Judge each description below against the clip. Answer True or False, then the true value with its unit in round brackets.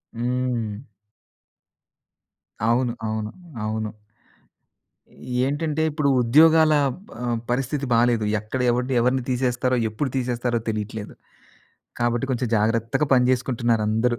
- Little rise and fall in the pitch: True (2.3 semitones)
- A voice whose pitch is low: True (120 Hz)